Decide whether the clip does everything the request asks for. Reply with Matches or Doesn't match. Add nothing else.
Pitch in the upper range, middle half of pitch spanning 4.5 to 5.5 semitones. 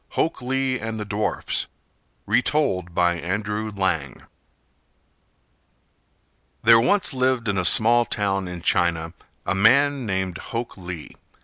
Doesn't match